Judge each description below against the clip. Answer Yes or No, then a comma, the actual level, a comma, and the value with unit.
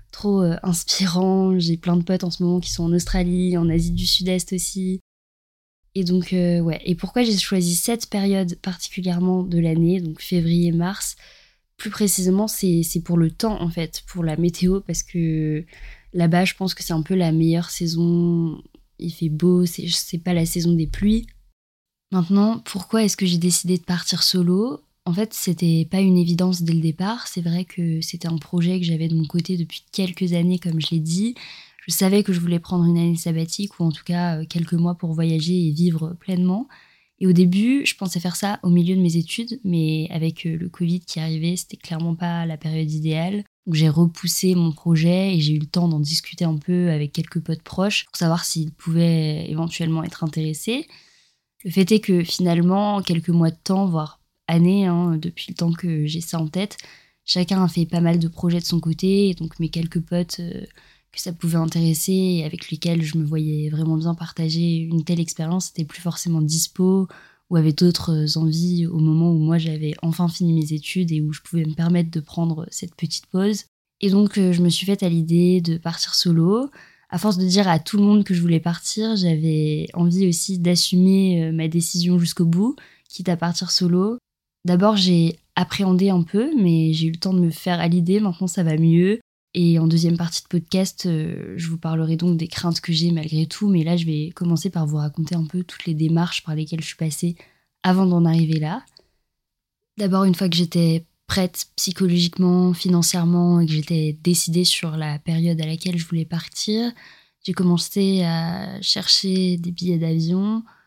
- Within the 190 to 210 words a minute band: Yes, average, 200 wpm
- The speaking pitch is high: No, medium, 175 Hz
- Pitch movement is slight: Yes, narrow, 2.0 semitones